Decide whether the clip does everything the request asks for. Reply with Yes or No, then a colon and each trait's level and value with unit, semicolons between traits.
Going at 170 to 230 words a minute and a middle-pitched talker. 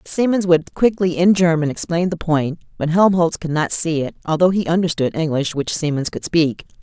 Yes: average, 195 wpm; medium, 165 Hz